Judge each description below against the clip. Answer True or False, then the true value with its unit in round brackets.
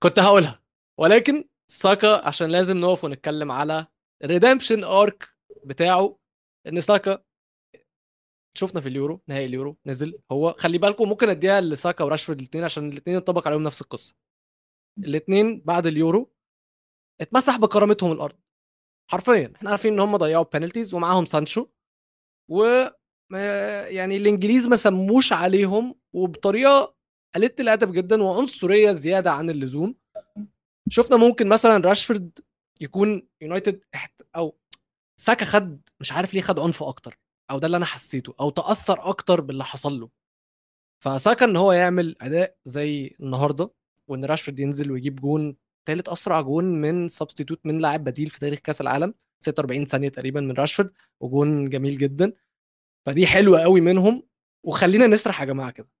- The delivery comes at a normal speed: False (140 wpm)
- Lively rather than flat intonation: True (5.7 semitones)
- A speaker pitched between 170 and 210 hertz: True (175 Hz)